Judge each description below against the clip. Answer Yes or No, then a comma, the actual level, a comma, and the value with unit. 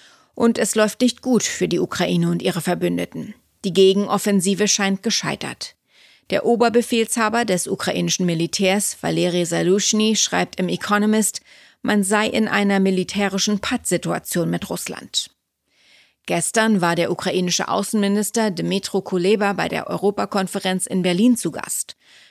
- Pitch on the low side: No, high, 195 Hz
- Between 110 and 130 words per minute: Yes, slow, 125 wpm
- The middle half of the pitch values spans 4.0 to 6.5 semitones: No, average, 2.9 semitones